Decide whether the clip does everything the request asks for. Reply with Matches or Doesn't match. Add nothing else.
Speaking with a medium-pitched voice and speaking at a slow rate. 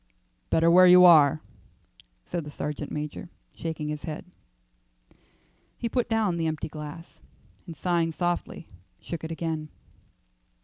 Matches